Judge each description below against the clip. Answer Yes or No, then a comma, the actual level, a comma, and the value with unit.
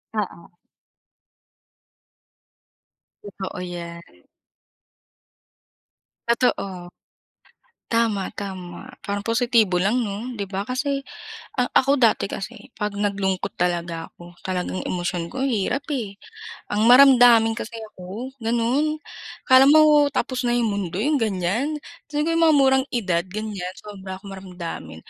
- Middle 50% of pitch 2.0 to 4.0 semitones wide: No, average, 5.2 semitones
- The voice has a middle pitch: No, high, 210 Hz